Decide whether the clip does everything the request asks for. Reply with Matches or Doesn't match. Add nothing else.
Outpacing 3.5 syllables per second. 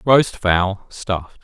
Doesn't match